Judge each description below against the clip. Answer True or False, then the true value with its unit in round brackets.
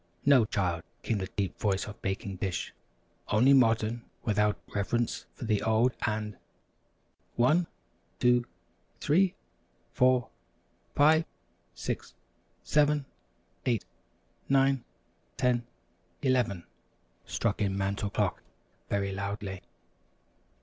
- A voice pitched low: True (110 Hz)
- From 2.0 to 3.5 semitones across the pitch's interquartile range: False (4.3 semitones)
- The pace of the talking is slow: True (100 wpm)